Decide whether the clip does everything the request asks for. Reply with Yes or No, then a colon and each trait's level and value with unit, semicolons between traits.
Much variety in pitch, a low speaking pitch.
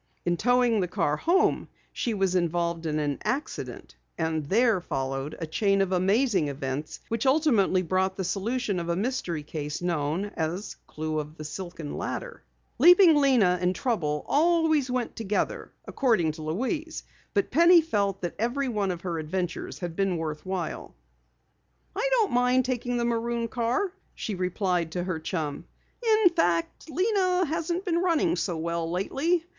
No: wide, 7.8 semitones; high, 195 Hz